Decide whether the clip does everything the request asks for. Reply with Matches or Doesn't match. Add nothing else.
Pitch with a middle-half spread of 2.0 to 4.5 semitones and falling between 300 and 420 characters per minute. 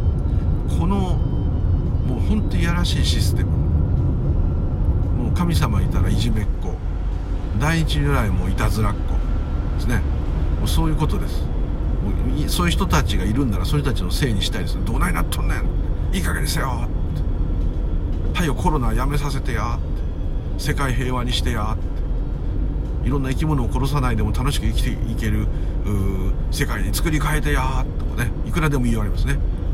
Matches